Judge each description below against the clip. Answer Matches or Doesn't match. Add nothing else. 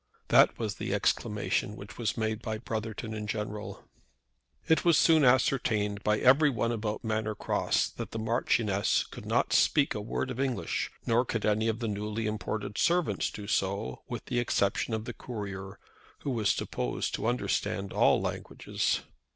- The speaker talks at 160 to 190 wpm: Matches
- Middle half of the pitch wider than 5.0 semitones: Doesn't match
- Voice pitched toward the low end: Matches